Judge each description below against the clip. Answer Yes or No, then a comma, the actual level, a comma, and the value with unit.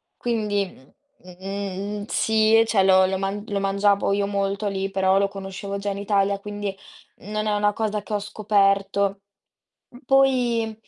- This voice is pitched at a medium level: No, high, 200 Hz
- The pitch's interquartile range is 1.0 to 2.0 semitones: Yes, narrow, 1.3 semitones